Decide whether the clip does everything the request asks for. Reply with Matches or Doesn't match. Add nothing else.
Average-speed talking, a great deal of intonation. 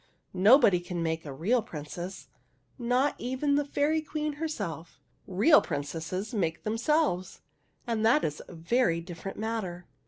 Matches